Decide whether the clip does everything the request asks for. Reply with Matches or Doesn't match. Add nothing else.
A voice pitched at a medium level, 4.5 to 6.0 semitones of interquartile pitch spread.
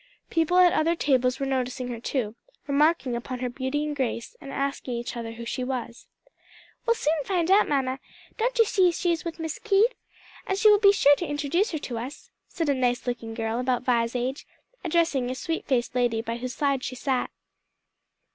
Doesn't match